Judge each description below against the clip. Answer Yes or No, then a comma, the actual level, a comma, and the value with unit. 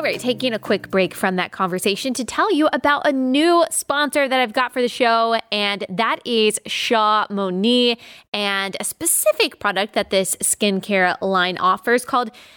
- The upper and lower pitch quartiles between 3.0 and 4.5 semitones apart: No, average, 4.9 semitones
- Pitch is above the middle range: Yes, high, 230 Hz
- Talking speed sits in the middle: Yes, average, 175 wpm